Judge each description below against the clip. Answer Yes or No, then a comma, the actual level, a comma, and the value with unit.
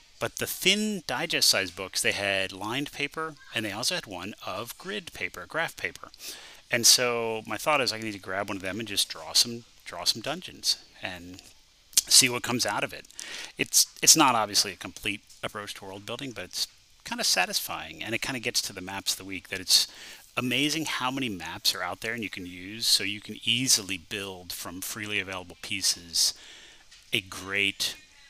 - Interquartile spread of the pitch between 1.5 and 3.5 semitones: No, average, 4.4 semitones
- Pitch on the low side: Yes, low, 105 Hz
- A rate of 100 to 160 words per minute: No, fast, 205 wpm